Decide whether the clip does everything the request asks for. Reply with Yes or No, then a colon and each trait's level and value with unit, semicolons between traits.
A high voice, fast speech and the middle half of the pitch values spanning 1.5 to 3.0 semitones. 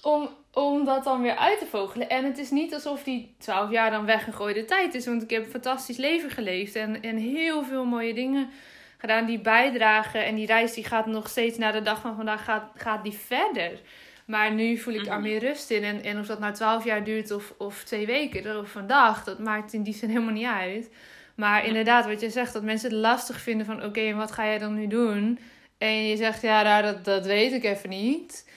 Yes: high, 225 Hz; fast, 235 wpm; narrow, 2.5 semitones